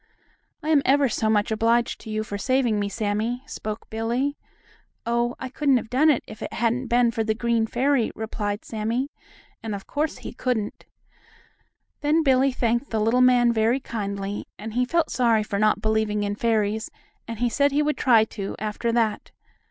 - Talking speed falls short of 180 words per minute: No, average, 185 wpm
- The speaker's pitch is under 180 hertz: No, high, 230 Hz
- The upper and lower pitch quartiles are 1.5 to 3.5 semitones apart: Yes, average, 2.7 semitones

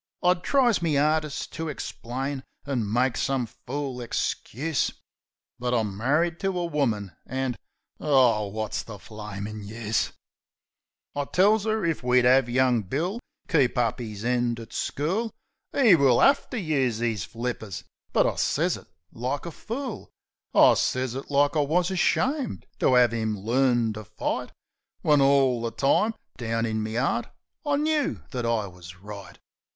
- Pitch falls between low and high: No, low, 130 Hz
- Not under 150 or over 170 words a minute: Yes, average, 155 wpm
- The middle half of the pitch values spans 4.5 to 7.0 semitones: Yes, wide, 5.6 semitones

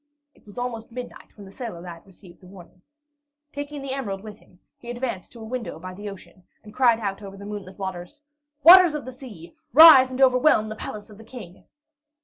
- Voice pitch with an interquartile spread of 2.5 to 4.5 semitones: No, average, 5.0 semitones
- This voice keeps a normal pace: No, fast, 210 wpm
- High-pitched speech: Yes, high, 215 Hz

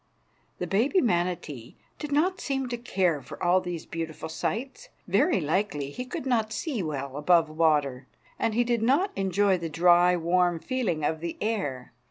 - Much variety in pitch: Yes, wide, 6.9 semitones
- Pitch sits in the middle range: Yes, medium, 180 Hz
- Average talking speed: Yes, average, 170 wpm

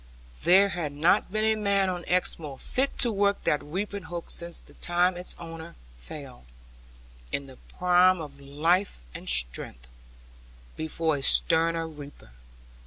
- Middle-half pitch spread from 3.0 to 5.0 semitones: Yes, average, 4.3 semitones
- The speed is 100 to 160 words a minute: Yes, average, 145 wpm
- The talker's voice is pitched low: No, medium, 170 Hz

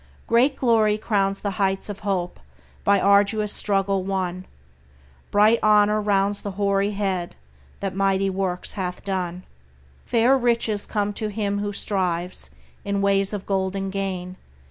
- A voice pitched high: Yes, high, 200 Hz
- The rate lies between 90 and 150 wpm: Yes, average, 140 wpm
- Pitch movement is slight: Yes, narrow, 1.4 semitones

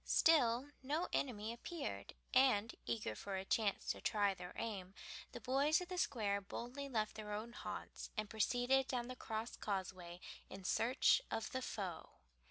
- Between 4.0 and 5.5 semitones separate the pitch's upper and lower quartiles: Yes, average, 4.5 semitones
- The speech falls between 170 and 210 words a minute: No, average, 160 wpm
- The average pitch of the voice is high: Yes, high, 225 Hz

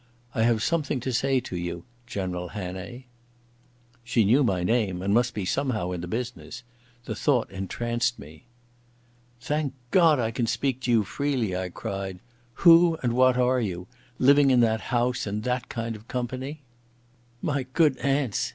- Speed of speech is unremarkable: Yes, average, 160 wpm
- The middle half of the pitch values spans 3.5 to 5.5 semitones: Yes, average, 4.6 semitones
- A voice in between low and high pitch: No, low, 120 Hz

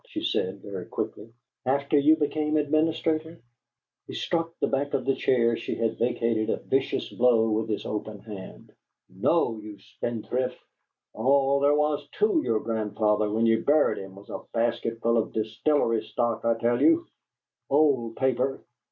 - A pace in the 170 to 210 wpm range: No, average, 160 wpm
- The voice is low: Yes, low, 120 Hz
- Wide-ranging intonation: No, average, 4.7 semitones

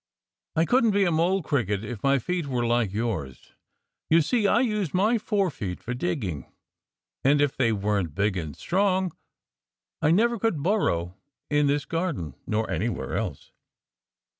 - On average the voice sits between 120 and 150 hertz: Yes, medium, 140 Hz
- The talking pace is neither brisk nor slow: Yes, average, 155 wpm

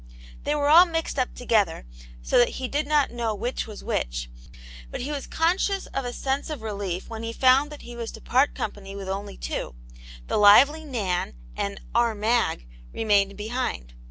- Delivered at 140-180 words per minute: No, average, 195 wpm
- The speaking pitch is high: Yes, high, 235 Hz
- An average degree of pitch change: No, wide, 5.7 semitones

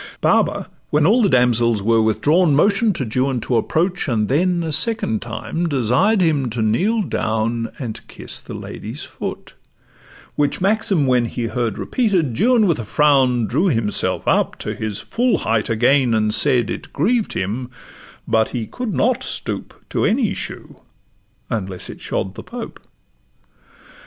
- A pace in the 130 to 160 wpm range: Yes, average, 155 wpm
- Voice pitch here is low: Yes, low, 130 Hz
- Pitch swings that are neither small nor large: No, wide, 8.4 semitones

